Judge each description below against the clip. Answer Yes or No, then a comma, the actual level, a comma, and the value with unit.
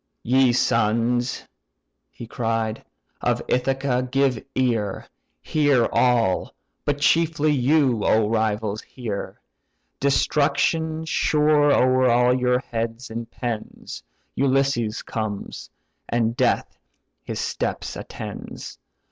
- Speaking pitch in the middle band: No, low, 125 Hz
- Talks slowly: Yes, slow, 95 wpm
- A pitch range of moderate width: Yes, average, 3.2 semitones